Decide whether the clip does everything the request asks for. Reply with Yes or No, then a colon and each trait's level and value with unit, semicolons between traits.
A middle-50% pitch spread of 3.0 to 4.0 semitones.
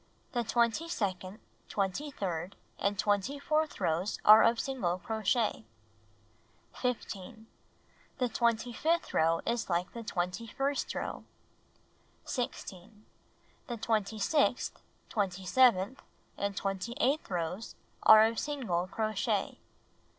No: average, 4.5 semitones